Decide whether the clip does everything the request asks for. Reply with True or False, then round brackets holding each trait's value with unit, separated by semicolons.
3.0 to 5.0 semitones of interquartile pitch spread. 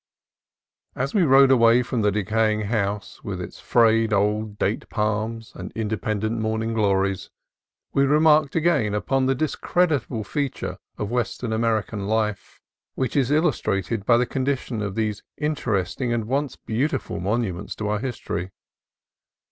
True (3.9 semitones)